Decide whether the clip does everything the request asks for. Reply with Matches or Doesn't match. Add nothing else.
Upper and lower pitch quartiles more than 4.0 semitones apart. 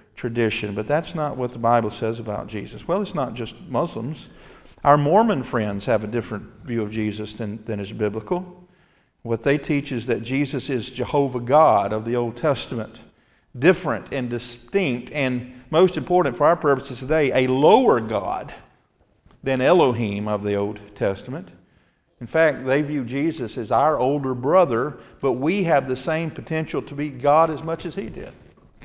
Matches